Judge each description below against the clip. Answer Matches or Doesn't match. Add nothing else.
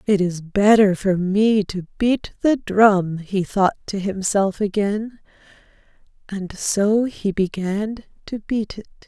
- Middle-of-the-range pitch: Doesn't match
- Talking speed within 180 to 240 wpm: Doesn't match